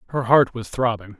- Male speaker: Yes, male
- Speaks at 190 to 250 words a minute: Yes, average, 200 wpm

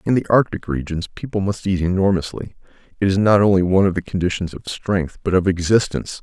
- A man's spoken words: Yes, male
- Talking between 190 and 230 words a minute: Yes, average, 200 wpm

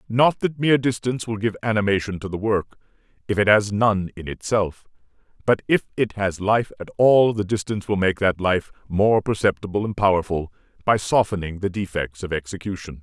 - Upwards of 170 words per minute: Yes, average, 180 wpm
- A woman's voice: No, male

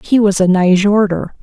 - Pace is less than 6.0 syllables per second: Yes, 4.8 syllables/s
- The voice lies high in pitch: Yes, high, 195 Hz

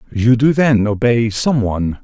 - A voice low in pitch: Yes, low, 115 Hz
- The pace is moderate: Yes, average, 175 wpm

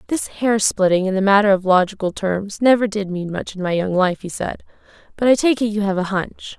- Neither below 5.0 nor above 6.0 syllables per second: Yes, 5.4 syllables/s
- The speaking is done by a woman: Yes, female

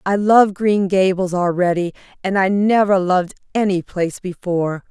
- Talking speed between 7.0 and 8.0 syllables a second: No, 5.0 syllables/s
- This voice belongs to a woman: Yes, female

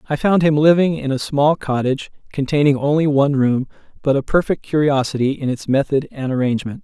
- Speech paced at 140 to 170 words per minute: No, average, 185 wpm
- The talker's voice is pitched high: No, medium, 140 Hz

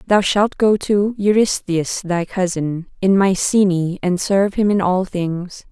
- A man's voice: No, female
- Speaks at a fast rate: No, average, 160 wpm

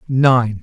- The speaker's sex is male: Yes, male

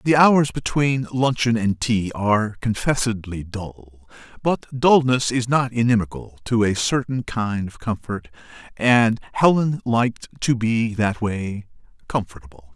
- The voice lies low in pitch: Yes, low, 115 Hz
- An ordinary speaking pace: No, slow, 130 wpm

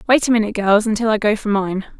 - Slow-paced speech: No, fast, 270 wpm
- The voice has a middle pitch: No, high, 215 Hz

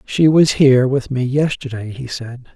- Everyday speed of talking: Yes, average, 190 wpm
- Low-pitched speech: Yes, low, 130 Hz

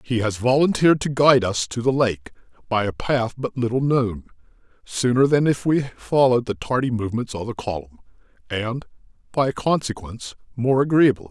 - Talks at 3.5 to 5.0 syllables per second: No, 5.4 syllables/s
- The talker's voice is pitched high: No, low, 120 Hz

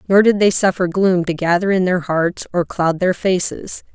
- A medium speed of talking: No, fast, 215 wpm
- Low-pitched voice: No, medium, 180 Hz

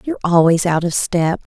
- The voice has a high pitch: No, medium, 175 Hz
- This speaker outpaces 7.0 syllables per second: No, 5.5 syllables/s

